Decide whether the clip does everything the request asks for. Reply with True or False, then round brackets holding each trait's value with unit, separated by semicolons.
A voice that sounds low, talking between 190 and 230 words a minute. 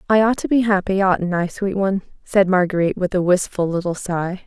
False (190 Hz; 200 wpm)